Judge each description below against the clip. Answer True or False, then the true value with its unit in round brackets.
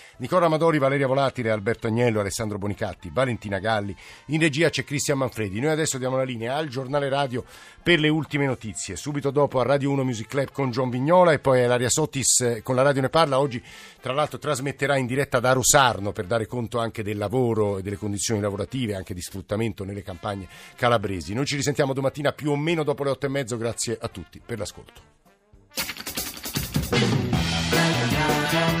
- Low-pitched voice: True (130 Hz)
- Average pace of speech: False (180 wpm)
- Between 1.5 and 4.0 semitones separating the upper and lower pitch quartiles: False (4.7 semitones)